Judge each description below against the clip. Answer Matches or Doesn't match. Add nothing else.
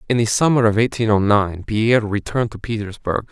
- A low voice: Matches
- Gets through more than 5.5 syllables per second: Matches